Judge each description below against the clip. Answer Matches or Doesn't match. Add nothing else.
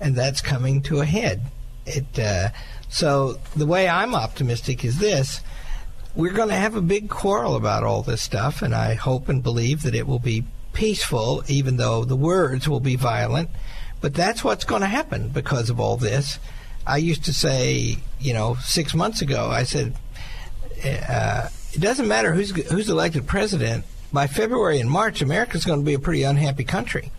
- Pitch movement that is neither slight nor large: Matches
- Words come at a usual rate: Matches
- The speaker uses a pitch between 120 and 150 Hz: Matches